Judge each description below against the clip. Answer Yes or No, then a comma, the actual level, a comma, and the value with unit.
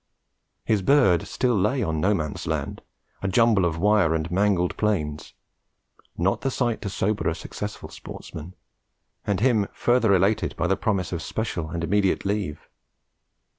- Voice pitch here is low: Yes, low, 100 Hz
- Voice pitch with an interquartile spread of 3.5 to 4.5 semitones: Yes, average, 3.9 semitones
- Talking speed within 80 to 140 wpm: No, average, 155 wpm